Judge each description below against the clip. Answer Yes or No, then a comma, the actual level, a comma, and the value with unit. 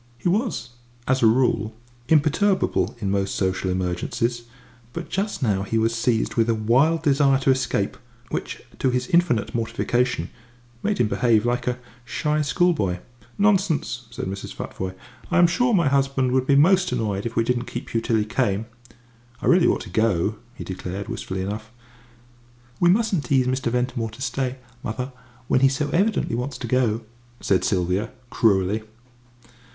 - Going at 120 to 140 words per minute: No, average, 165 wpm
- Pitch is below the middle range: Yes, low, 125 Hz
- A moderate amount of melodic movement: Yes, average, 4.6 semitones